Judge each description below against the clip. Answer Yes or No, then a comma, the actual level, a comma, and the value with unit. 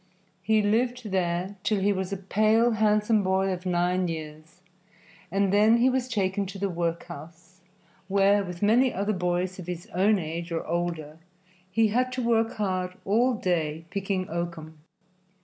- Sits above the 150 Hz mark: Yes, high, 190 Hz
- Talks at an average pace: Yes, average, 160 wpm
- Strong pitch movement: No, average, 3.5 semitones